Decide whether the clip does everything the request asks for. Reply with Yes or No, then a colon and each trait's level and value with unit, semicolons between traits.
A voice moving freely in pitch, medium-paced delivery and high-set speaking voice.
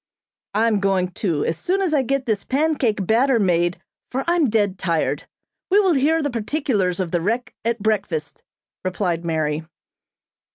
Yes: wide, 7.1 semitones; average, 160 wpm; high, 215 Hz